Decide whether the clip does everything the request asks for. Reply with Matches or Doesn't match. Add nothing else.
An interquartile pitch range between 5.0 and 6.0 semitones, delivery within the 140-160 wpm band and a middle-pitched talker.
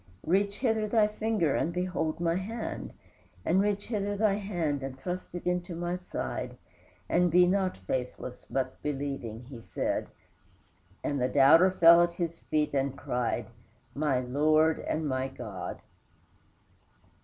Matches